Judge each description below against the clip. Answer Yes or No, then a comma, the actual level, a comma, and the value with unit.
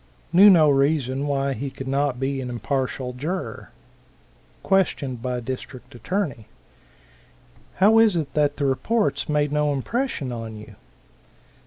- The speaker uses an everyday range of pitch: Yes, average, 3.6 semitones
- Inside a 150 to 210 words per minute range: No, slow, 135 wpm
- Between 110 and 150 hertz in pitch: Yes, medium, 140 Hz